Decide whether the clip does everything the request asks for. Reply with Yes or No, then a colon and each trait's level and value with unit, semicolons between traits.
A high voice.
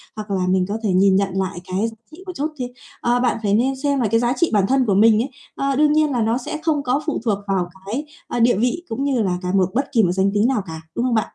Yes: high, 230 Hz